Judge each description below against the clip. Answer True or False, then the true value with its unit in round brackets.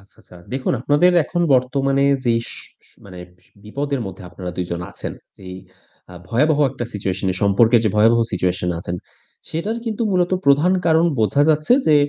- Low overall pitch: True (125 Hz)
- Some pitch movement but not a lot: False (7.5 semitones)